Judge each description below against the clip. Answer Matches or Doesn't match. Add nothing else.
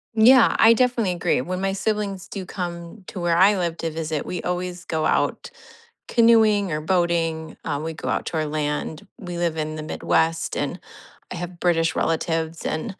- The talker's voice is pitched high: Doesn't match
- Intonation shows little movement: Doesn't match